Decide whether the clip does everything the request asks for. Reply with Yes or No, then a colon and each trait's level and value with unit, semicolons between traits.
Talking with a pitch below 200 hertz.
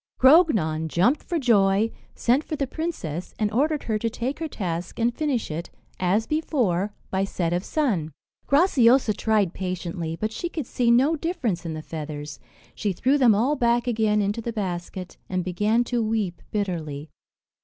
No: high, 215 Hz